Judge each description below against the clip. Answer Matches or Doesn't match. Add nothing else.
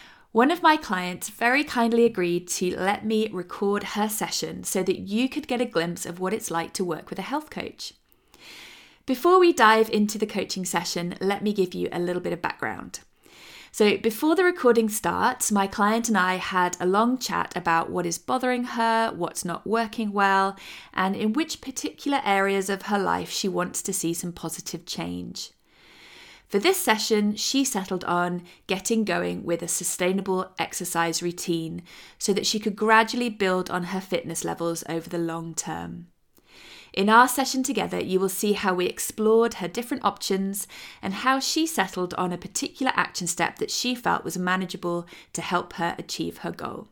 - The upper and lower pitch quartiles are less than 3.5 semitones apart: Doesn't match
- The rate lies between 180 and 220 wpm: Matches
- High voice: Matches